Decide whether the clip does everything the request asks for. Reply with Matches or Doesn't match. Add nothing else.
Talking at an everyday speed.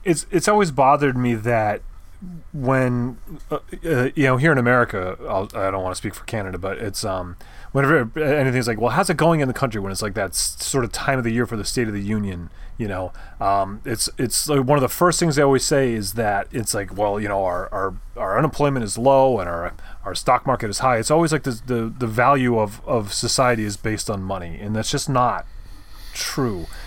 Doesn't match